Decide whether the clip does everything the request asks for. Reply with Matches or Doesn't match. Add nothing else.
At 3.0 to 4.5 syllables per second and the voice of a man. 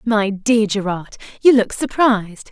Doesn't match